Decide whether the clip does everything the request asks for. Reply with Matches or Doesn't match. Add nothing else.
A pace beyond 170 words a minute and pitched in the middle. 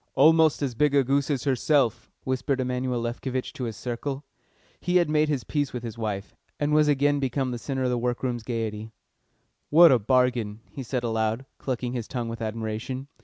Doesn't match